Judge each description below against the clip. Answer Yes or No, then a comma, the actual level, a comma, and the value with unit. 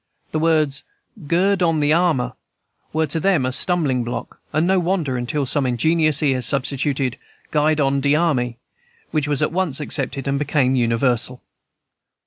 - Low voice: No, medium, 145 Hz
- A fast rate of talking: No, average, 155 wpm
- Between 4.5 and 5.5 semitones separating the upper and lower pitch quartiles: No, average, 3.7 semitones